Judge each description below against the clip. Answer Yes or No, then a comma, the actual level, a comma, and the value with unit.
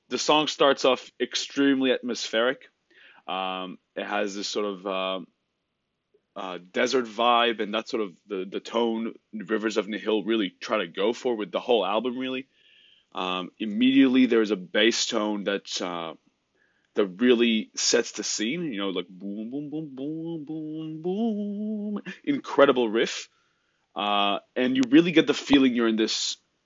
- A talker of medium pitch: No, low, 120 Hz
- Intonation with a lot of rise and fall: Yes, wide, 6.5 semitones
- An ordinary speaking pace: Yes, average, 160 wpm